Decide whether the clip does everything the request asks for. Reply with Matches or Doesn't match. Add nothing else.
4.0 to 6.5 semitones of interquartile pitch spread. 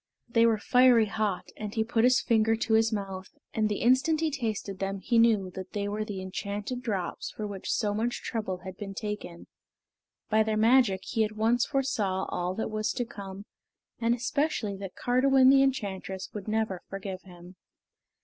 Doesn't match